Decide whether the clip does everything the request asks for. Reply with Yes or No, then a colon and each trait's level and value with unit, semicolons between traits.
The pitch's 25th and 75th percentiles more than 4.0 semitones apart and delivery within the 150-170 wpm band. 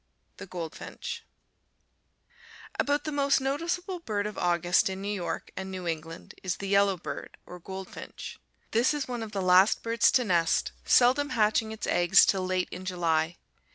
Yes: average, 5.2 semitones; average, 160 wpm